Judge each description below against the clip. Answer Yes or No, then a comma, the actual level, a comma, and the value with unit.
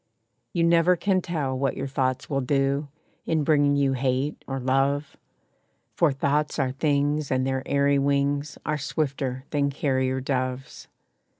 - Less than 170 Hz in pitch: Yes, medium, 140 Hz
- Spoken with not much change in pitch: Yes, narrow, 1.9 semitones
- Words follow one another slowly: No, average, 145 wpm